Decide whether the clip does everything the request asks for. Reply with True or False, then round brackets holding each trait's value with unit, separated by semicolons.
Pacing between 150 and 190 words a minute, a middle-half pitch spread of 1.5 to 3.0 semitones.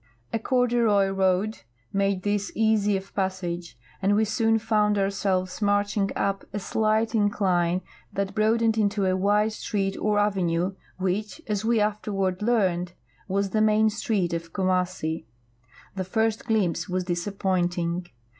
False (135 wpm; 2.5 semitones)